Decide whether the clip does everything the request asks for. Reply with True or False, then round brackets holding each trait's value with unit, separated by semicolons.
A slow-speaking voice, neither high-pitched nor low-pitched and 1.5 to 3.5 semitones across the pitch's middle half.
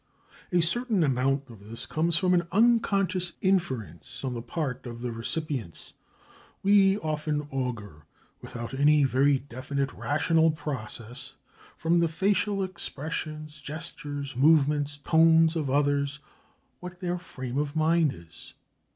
False (125 wpm; 150 Hz; 4.4 semitones)